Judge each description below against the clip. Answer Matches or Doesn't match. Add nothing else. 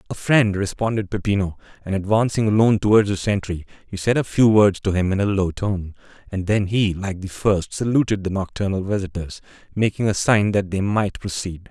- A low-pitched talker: Matches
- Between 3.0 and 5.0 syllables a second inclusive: Doesn't match